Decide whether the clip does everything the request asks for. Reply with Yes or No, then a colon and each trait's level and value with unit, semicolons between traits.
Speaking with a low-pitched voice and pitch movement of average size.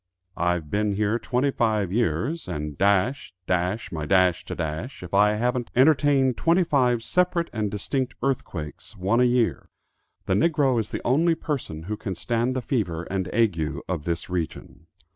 No: low, 105 Hz; wide, 6.2 semitones